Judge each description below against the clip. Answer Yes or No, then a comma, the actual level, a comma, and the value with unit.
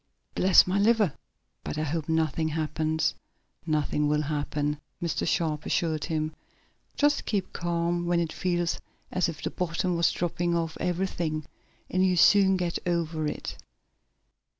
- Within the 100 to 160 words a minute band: Yes, average, 150 wpm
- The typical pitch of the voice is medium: Yes, medium, 170 Hz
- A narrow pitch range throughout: Yes, narrow, 2.3 semitones